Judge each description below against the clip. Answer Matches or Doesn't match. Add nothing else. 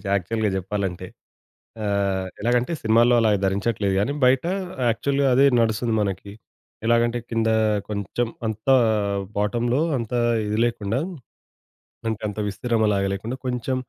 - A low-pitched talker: Matches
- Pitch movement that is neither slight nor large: Matches